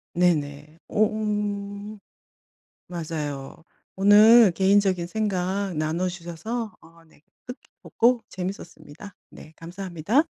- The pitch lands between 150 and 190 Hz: Yes, medium, 185 Hz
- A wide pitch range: No, average, 4.0 semitones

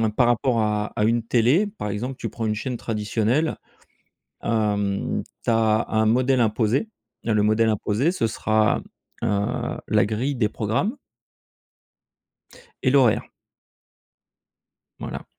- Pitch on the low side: Yes, low, 115 Hz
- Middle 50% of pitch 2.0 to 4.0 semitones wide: Yes, average, 2.8 semitones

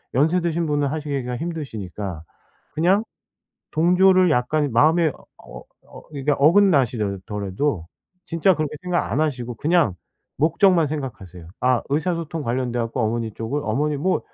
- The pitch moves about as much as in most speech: No, wide, 5.8 semitones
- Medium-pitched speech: Yes, medium, 145 Hz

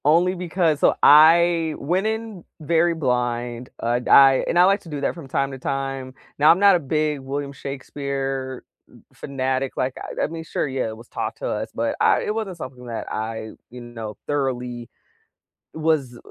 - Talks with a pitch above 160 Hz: No, medium, 140 Hz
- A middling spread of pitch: Yes, average, 4.1 semitones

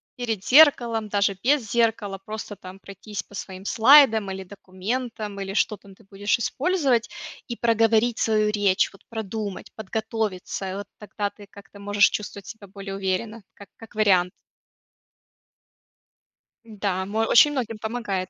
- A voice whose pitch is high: Yes, high, 210 Hz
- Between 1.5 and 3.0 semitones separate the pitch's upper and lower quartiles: Yes, narrow, 2.6 semitones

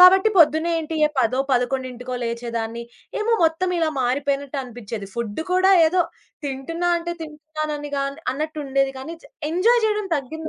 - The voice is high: Yes, very high, 290 Hz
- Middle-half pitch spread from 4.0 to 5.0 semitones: Yes, average, 4.6 semitones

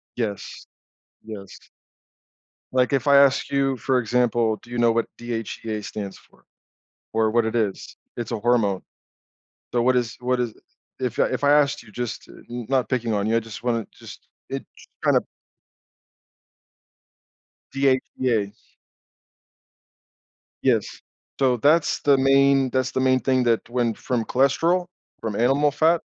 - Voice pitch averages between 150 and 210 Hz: No, low, 125 Hz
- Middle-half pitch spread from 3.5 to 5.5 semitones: No, average, 2.9 semitones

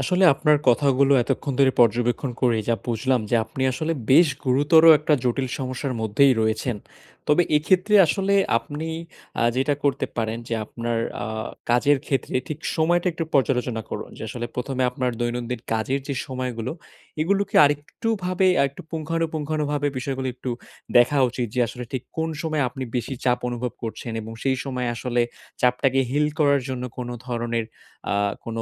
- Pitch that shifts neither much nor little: Yes, average, 3.5 semitones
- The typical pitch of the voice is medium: No, low, 130 Hz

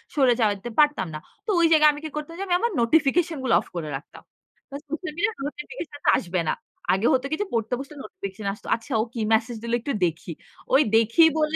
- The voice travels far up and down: Yes, wide, 5.8 semitones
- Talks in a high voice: Yes, very high, 270 Hz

